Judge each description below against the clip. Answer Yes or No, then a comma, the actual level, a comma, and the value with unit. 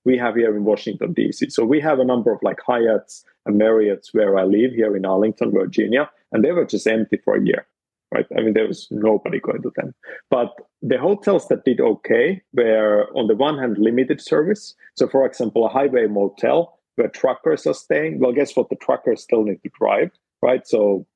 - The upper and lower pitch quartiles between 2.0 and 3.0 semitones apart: Yes, narrow, 2.6 semitones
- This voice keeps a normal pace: No, fast, 210 wpm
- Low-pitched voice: Yes, low, 110 Hz